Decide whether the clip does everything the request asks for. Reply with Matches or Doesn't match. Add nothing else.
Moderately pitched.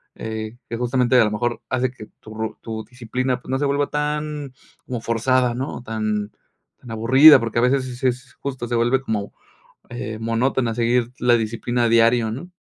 Doesn't match